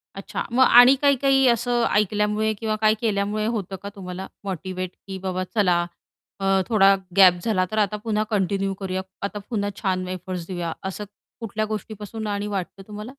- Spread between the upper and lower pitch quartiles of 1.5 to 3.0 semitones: Yes, narrow, 2.5 semitones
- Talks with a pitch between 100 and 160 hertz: No, high, 205 Hz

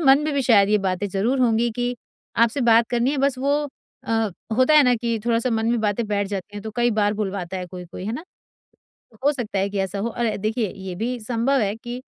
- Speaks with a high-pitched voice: Yes, high, 225 Hz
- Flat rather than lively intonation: No, average, 3.3 semitones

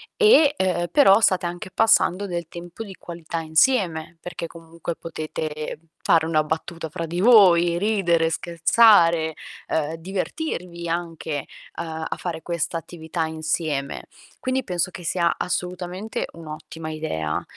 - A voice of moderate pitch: Yes, medium, 170 Hz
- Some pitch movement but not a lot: No, narrow, 2.2 semitones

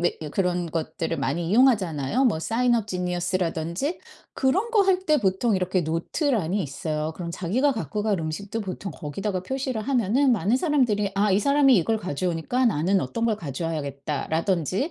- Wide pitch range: Yes, wide, 6.5 semitones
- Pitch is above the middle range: Yes, high, 195 Hz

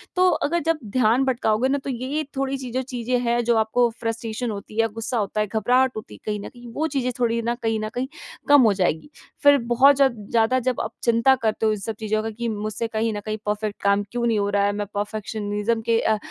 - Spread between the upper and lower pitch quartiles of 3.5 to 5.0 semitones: No, average, 2.8 semitones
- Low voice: No, high, 230 Hz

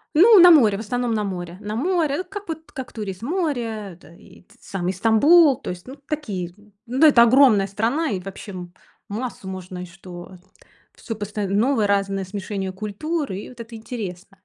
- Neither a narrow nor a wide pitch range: No, wide, 6.0 semitones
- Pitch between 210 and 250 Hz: Yes, high, 215 Hz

